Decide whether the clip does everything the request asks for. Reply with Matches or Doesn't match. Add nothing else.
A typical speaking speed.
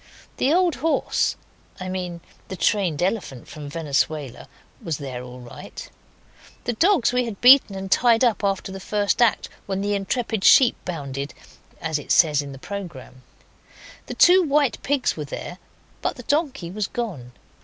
Matches